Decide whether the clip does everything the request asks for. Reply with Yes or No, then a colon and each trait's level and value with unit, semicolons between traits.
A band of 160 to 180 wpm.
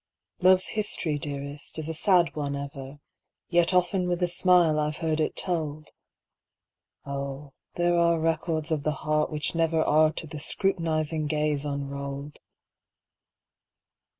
No: slow, 135 wpm